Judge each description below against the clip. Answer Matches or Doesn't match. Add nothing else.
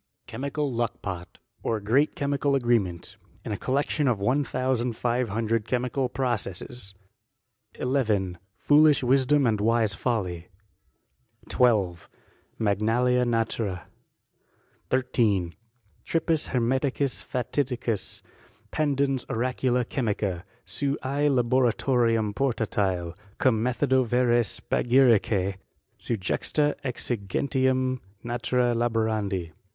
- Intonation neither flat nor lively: Matches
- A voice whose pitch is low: Matches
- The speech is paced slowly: Matches